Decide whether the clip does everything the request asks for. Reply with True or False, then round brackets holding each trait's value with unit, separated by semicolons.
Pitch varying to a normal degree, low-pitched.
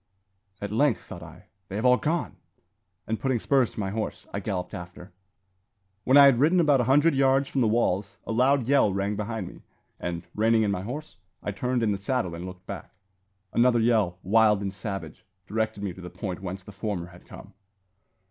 True (4.9 semitones; 110 Hz)